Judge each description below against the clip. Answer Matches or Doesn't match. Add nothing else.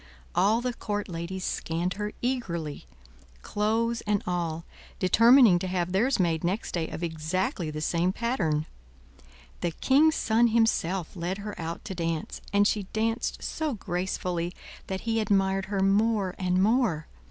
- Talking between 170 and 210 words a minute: Doesn't match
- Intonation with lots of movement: Doesn't match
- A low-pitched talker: Doesn't match